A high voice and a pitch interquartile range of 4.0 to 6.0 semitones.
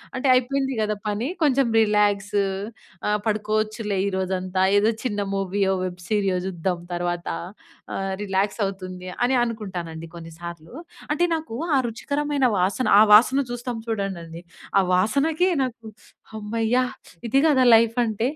Yes: high, 210 Hz; average, 4.4 semitones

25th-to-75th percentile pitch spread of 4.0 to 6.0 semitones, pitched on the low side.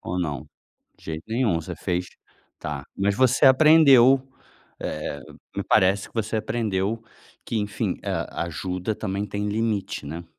Yes: average, 4.5 semitones; low, 100 Hz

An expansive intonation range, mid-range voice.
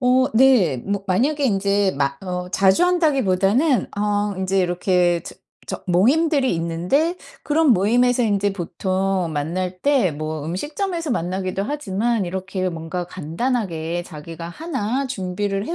No: wide, 6.0 semitones; high, 195 Hz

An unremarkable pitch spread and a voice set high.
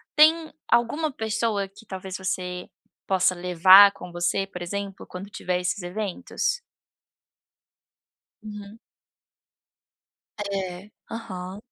Yes: average, 3.2 semitones; high, 195 Hz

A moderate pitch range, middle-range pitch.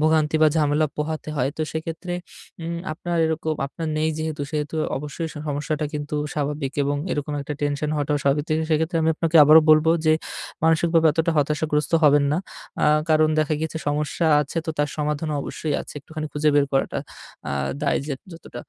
No: narrow, 1.4 semitones; medium, 155 Hz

